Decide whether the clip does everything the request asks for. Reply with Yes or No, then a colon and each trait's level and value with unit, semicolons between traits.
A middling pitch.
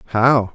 No: low, 110 Hz